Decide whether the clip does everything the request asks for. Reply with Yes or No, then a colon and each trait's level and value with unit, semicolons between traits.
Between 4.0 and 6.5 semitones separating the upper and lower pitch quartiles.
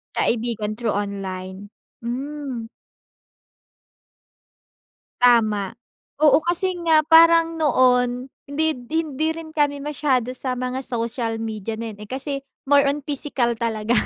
Yes: average, 4.6 semitones